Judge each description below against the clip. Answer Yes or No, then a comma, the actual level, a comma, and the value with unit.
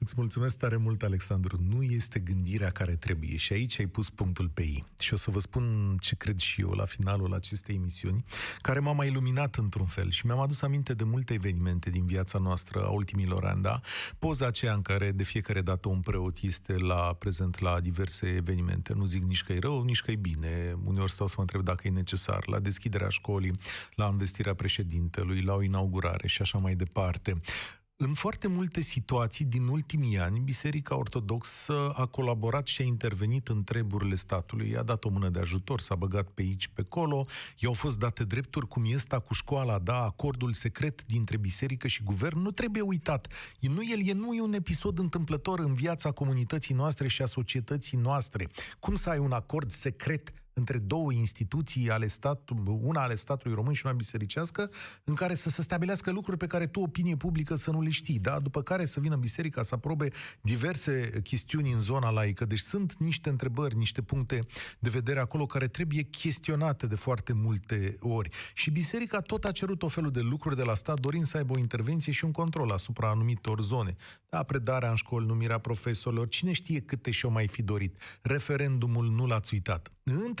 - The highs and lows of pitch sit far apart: Yes, wide, 6.1 semitones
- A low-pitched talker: Yes, low, 120 Hz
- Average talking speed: No, fast, 195 wpm